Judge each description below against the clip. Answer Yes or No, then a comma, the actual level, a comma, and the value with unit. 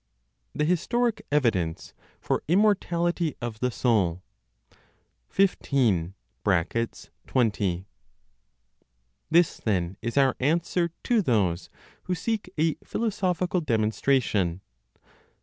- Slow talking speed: Yes, slow, 85 wpm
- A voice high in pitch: No, medium, 140 Hz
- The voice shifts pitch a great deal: Yes, wide, 8.8 semitones